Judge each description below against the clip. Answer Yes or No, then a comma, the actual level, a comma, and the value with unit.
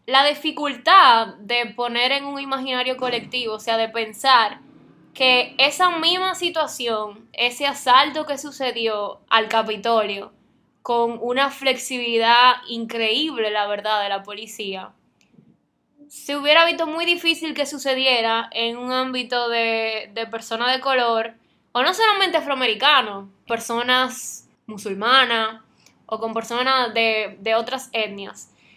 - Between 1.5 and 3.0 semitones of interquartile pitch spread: No, average, 3.5 semitones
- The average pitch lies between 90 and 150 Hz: No, high, 245 Hz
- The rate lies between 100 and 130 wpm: Yes, slow, 125 wpm